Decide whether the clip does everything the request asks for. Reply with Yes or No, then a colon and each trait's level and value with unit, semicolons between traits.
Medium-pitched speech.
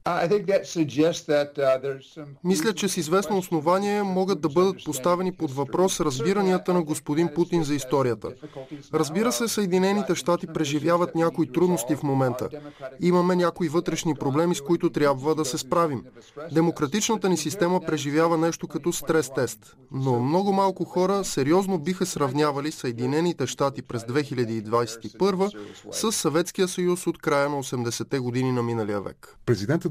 Yes: medium, 160 Hz